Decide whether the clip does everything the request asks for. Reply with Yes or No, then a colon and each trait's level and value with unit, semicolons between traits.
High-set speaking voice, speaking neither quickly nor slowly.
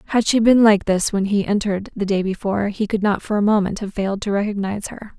No: high, 205 Hz; fast, 255 wpm